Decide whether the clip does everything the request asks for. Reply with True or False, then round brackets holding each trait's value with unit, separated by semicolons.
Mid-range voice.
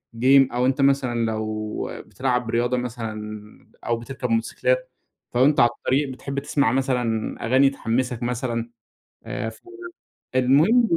False (125 Hz)